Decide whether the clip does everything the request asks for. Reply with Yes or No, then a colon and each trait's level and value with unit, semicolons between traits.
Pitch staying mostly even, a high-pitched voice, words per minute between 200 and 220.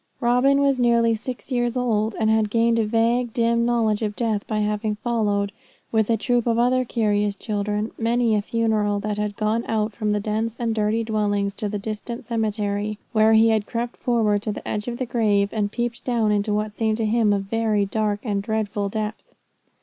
Yes: narrow, 1.9 semitones; high, 220 Hz; fast, 205 wpm